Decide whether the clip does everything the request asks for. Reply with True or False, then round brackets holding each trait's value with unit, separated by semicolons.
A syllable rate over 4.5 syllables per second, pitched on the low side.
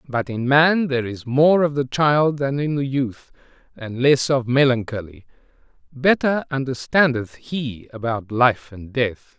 False (4.1 syllables/s; 130 Hz)